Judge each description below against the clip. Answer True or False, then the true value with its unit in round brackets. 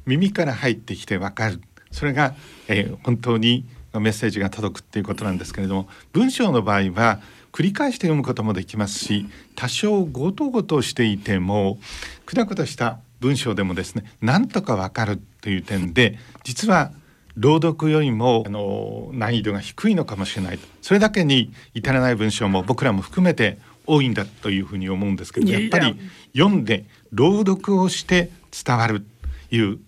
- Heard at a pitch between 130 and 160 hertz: False (115 Hz)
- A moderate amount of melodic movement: False (7.0 semitones)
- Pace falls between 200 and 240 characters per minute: False (350 characters per minute)